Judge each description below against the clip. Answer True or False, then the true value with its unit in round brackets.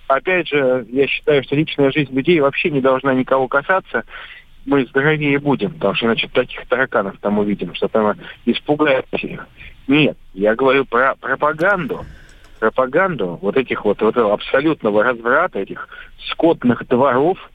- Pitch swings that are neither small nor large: True (4.4 semitones)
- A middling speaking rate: True (145 wpm)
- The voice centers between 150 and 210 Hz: False (135 Hz)